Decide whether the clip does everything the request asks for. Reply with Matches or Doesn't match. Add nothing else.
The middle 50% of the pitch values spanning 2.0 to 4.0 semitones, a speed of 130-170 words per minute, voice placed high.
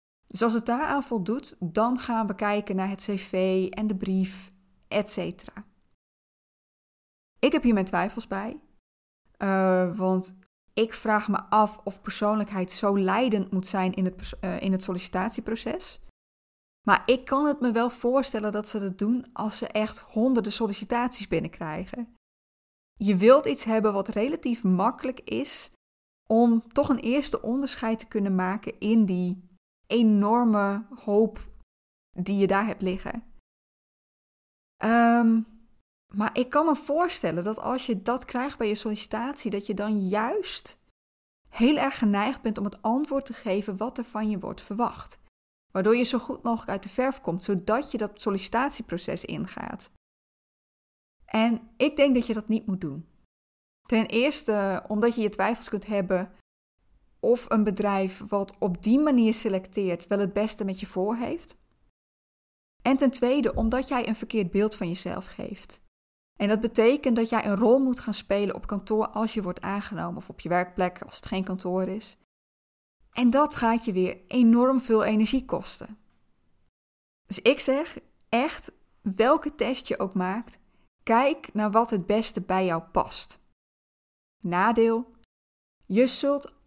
Matches